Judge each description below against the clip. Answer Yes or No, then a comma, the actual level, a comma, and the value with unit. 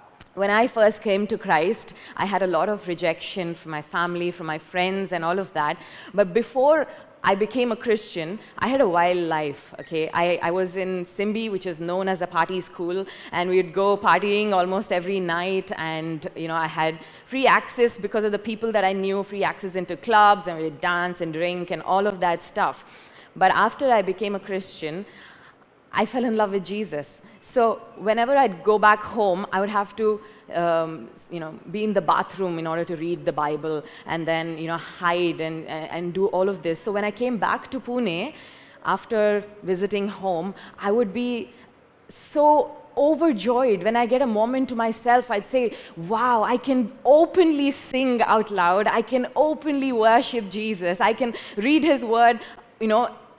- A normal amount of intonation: Yes, average, 4.7 semitones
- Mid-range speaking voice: No, high, 200 Hz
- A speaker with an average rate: Yes, average, 195 wpm